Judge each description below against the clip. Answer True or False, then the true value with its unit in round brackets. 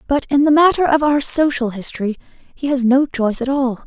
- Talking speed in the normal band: False (215 wpm)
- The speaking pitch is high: True (270 Hz)